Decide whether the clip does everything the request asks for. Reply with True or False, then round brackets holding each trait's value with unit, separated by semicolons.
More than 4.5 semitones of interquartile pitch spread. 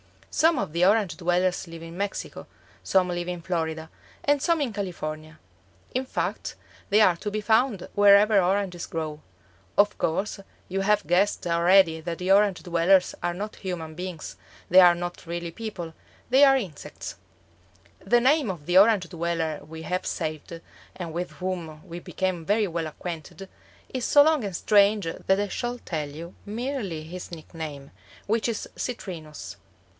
False (3.7 semitones)